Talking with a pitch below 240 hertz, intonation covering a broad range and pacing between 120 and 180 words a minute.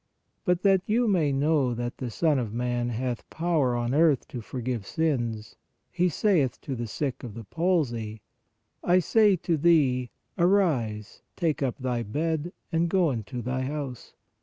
Yes: low, 135 Hz; wide, 5.7 semitones; average, 160 wpm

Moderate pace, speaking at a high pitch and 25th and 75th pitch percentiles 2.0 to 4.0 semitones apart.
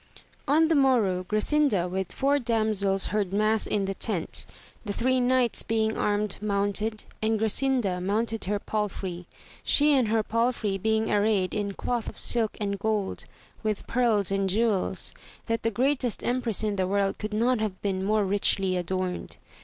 Yes: average, 165 wpm; high, 215 Hz; average, 2.8 semitones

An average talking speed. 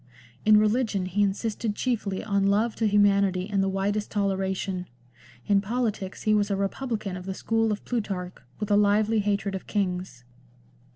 Yes: average, 165 wpm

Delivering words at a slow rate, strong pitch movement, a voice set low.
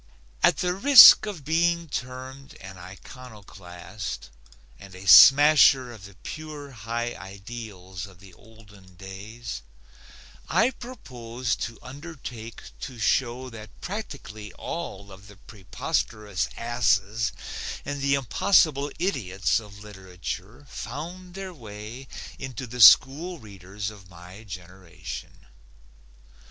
Yes: slow, 110 wpm; wide, 6.1 semitones; low, 115 Hz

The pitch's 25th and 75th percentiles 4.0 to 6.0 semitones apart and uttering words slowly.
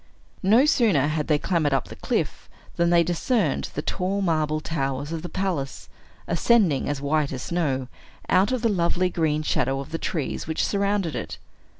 No: average, 4.4 semitones; average, 180 wpm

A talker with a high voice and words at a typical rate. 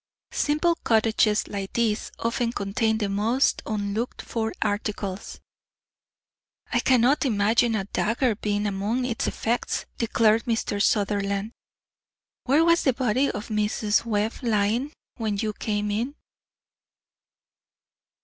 No: high, 220 Hz; slow, 115 wpm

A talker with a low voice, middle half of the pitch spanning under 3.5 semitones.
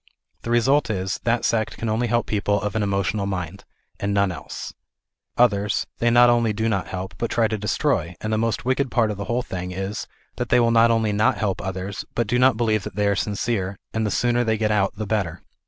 Yes: low, 110 Hz; average, 2.9 semitones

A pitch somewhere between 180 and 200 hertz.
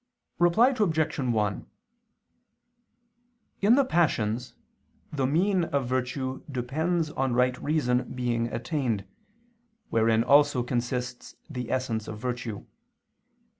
No: low, 130 Hz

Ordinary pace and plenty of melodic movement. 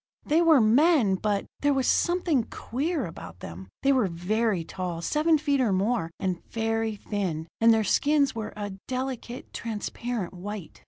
Yes: average, 160 wpm; wide, 6.0 semitones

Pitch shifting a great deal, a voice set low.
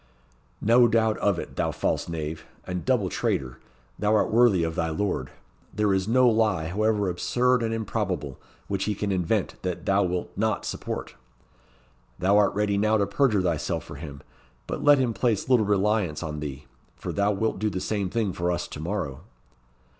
No: average, 3.9 semitones; low, 100 Hz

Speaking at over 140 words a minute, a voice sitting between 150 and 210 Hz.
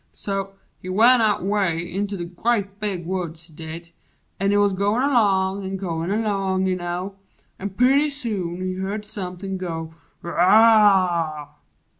Yes: average, 150 wpm; high, 190 Hz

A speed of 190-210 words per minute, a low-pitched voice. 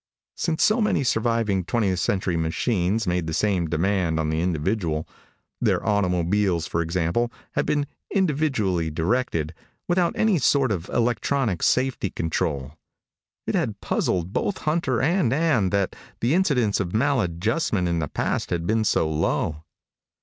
No: average, 140 wpm; low, 100 Hz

